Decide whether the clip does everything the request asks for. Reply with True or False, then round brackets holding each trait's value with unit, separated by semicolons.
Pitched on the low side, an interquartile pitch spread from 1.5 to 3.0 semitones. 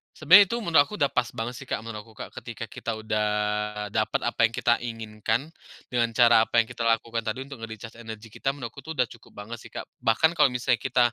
True (115 Hz; 2.4 semitones)